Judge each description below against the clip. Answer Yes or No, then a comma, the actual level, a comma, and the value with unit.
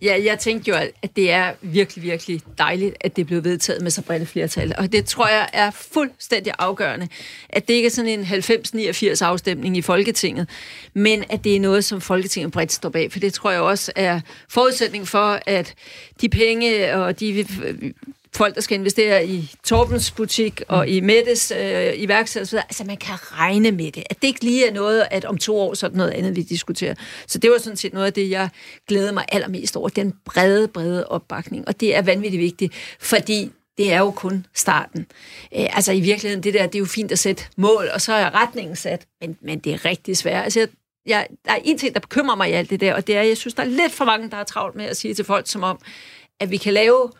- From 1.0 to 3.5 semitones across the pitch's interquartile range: Yes, average, 2.8 semitones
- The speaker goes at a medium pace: No, fast, 235 wpm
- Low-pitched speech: No, high, 200 Hz